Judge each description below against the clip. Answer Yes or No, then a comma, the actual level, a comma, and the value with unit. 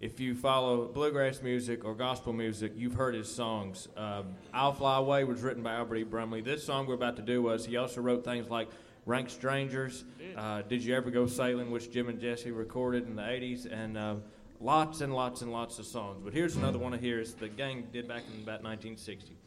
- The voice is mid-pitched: No, low, 120 Hz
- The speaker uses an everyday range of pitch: No, narrow, 2.1 semitones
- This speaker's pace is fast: Yes, fast, 225 wpm